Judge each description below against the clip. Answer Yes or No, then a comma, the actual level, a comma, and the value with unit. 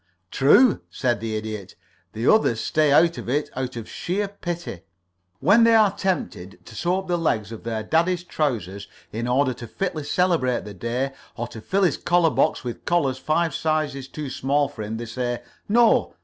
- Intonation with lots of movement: Yes, wide, 6.9 semitones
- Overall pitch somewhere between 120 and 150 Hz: Yes, medium, 140 Hz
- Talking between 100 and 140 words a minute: No, average, 190 wpm